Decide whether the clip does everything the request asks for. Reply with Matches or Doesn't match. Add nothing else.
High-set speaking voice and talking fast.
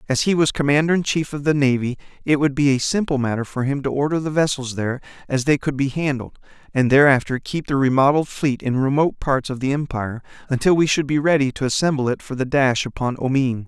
Doesn't match